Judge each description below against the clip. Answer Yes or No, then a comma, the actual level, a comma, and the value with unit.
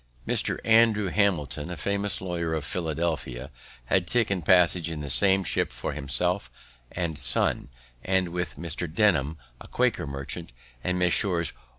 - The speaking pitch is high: No, very low, 85 Hz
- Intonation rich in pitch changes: No, average, 3.4 semitones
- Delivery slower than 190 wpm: Yes, average, 145 wpm